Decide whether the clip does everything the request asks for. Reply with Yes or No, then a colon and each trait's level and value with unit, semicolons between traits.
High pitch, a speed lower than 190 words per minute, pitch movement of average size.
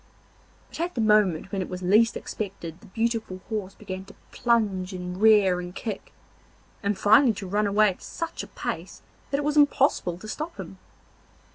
Yes: high, 205 Hz; average, 180 wpm; average, 3.6 semitones